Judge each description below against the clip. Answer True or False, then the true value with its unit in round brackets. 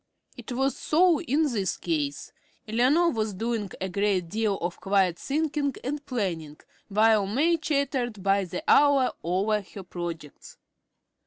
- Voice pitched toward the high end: True (215 Hz)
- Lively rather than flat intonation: True (6.7 semitones)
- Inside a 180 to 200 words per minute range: False (140 wpm)